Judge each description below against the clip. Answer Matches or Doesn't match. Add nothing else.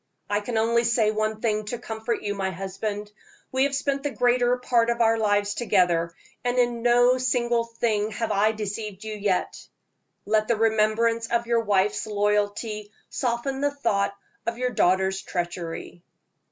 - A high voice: Matches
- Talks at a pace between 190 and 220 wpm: Doesn't match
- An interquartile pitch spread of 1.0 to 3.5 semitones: Matches